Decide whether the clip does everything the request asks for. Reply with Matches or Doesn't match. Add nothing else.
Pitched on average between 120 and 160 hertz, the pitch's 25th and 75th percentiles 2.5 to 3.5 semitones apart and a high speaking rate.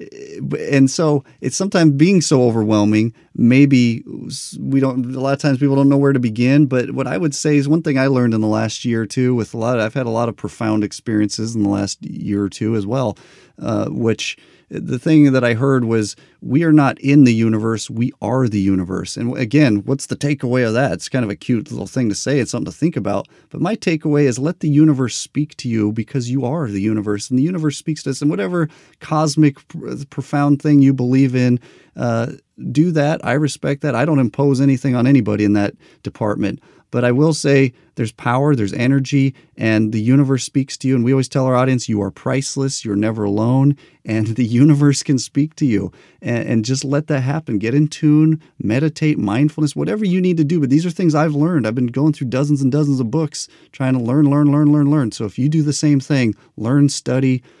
Doesn't match